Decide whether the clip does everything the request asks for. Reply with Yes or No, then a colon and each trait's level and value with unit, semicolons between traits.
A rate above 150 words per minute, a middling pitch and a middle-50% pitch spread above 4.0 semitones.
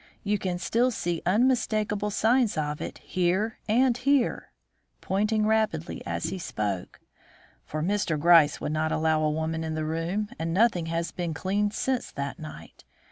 Yes: average, 160 wpm; medium, 180 Hz; average, 5.2 semitones